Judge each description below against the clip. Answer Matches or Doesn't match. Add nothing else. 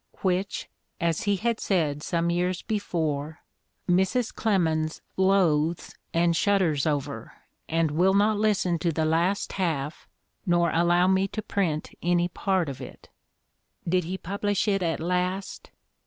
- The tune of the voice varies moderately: Matches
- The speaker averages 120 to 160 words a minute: Matches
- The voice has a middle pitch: Matches